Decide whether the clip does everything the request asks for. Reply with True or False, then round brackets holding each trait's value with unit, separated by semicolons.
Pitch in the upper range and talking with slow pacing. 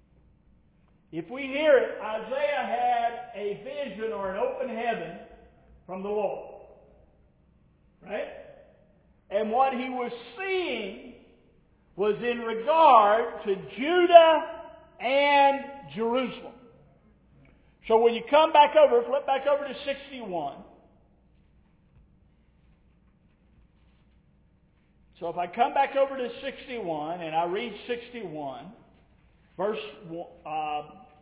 True (240 Hz; 100 wpm)